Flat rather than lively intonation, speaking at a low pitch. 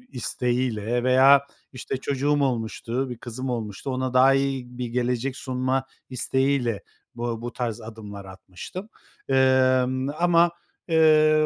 Yes: narrow, 2.1 semitones; low, 130 Hz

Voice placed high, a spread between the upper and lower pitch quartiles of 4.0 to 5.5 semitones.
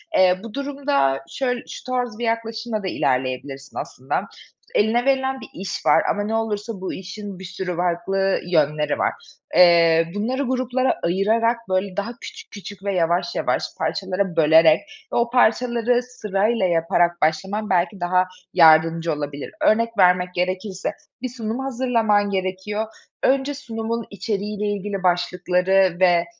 Yes: high, 195 Hz; average, 4.6 semitones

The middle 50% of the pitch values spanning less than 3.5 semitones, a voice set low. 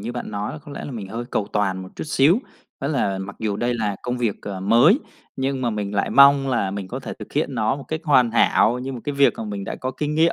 No: average, 5.1 semitones; low, 120 Hz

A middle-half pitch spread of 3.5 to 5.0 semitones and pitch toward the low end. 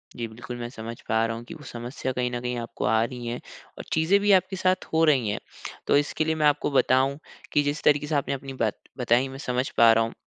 Yes: average, 3.9 semitones; low, 130 Hz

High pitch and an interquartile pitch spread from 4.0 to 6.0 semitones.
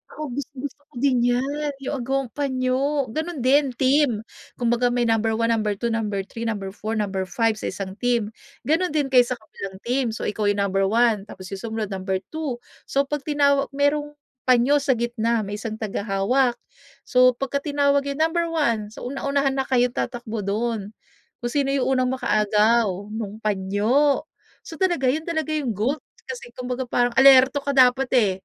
Yes: high, 245 Hz; average, 4.4 semitones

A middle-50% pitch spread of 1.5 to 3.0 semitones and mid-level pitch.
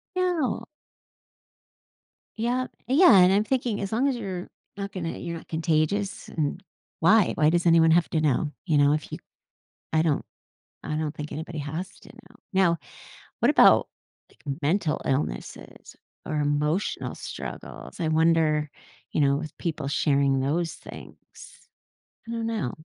No: average, 4.7 semitones; medium, 165 Hz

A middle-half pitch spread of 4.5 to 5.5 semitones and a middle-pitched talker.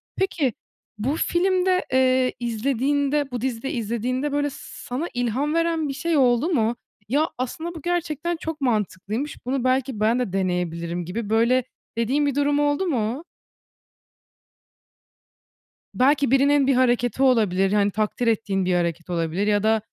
No: average, 5.0 semitones; very high, 255 Hz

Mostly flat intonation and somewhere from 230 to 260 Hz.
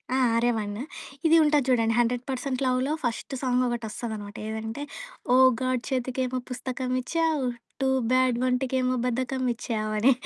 Yes: narrow, 1.7 semitones; very high, 255 Hz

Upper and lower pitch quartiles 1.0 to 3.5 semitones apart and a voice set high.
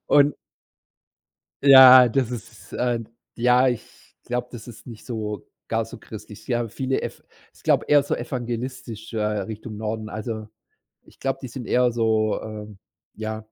No: narrow, 2.6 semitones; low, 120 Hz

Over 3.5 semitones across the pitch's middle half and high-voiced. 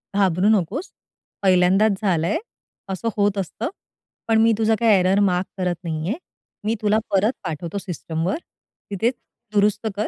No: average, 3.2 semitones; high, 195 Hz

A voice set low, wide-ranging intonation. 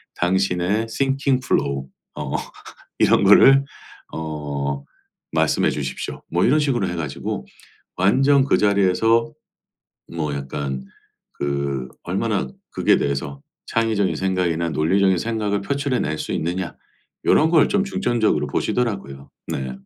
Yes: very low, 95 Hz; wide, 8.3 semitones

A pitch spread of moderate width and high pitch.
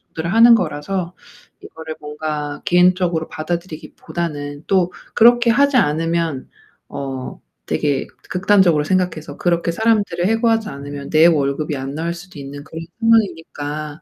No: average, 4.1 semitones; medium, 165 Hz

